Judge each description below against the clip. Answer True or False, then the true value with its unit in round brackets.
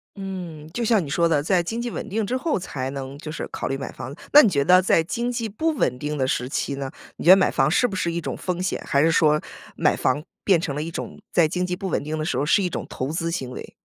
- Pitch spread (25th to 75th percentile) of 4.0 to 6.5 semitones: True (4.9 semitones)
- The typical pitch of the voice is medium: True (170 Hz)